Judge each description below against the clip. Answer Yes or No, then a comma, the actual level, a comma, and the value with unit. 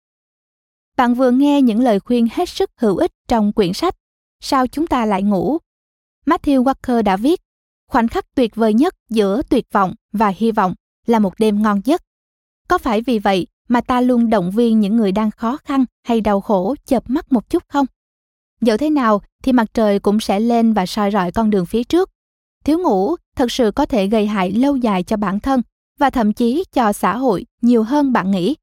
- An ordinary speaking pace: Yes, average, 210 wpm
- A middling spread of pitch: Yes, average, 4.3 semitones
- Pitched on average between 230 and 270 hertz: Yes, high, 235 Hz